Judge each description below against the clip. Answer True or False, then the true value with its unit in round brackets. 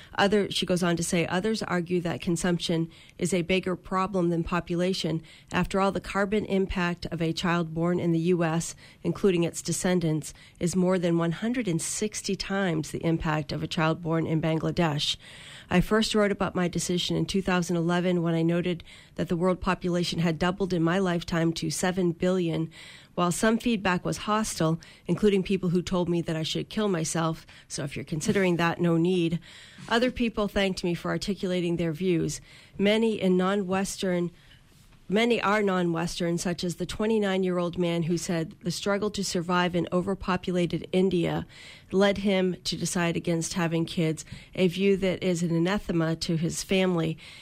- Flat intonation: True (2.2 semitones)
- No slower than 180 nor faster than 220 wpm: False (170 wpm)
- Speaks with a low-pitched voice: False (175 Hz)